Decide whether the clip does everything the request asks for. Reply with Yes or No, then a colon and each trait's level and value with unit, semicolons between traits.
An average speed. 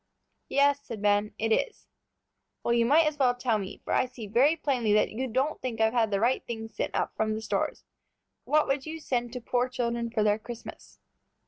No: fast, 215 wpm